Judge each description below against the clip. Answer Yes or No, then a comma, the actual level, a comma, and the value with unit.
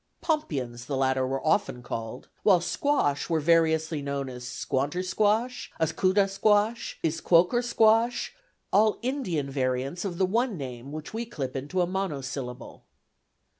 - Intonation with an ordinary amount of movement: No, wide, 7.4 semitones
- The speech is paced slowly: Yes, slow, 125 wpm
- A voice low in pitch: No, medium, 165 Hz